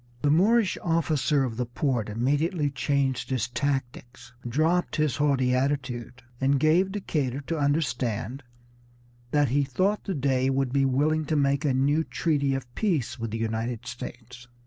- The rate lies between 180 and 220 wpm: No, average, 155 wpm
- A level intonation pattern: No, average, 3.5 semitones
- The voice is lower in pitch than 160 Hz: Yes, low, 135 Hz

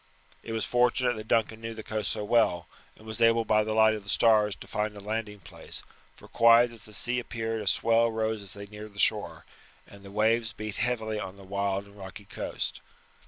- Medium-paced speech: No, fast, 220 wpm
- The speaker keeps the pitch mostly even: Yes, narrow, 1.8 semitones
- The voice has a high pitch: No, low, 110 Hz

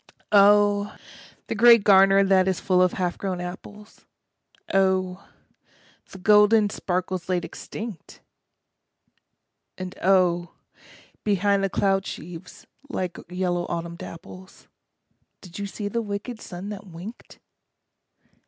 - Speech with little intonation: Yes, narrow, 2.1 semitones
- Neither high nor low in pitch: No, high, 195 Hz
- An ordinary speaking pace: No, slow, 115 wpm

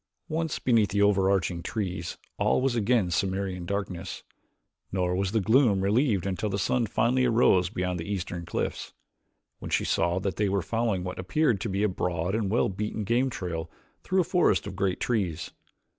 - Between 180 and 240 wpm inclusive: Yes, average, 185 wpm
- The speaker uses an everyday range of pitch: Yes, average, 3.8 semitones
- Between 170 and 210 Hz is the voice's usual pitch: No, low, 100 Hz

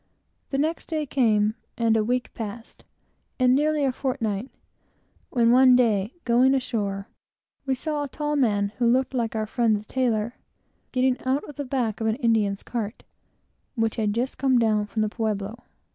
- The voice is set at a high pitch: Yes, high, 235 Hz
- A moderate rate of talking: Yes, average, 175 wpm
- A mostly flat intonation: No, average, 3.3 semitones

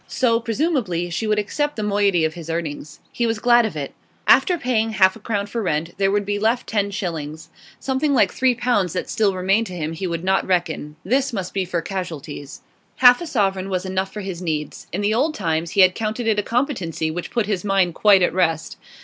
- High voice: Yes, high, 195 Hz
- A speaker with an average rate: No, fast, 225 wpm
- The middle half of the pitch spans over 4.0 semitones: Yes, average, 4.5 semitones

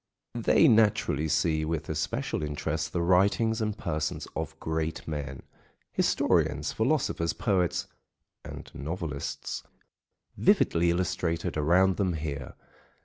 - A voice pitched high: No, very low, 85 Hz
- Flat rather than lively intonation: No, average, 3.2 semitones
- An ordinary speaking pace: No, slow, 100 wpm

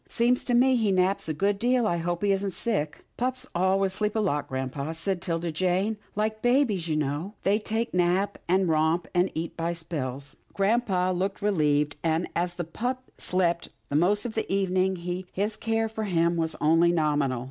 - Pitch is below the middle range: No, medium, 185 Hz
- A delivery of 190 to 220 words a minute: Yes, average, 195 wpm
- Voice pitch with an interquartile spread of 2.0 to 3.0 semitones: No, average, 4.3 semitones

